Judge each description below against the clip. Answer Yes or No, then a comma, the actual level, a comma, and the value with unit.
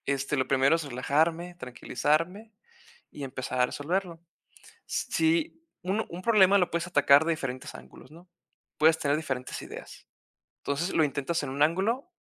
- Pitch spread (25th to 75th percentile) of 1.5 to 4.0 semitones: No, average, 4.5 semitones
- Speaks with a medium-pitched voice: Yes, medium, 160 Hz